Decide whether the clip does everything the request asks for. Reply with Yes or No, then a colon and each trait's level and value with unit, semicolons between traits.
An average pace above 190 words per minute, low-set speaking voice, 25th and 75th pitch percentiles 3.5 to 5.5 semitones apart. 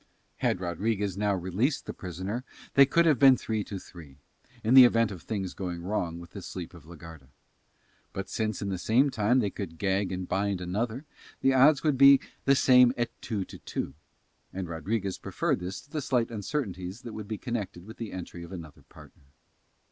Yes: average, 200 wpm; low, 100 Hz; average, 5.0 semitones